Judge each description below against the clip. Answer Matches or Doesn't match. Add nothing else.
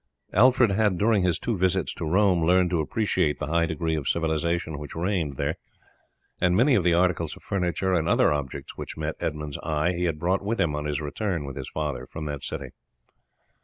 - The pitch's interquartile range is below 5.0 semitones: Matches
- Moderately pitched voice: Doesn't match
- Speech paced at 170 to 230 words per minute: Matches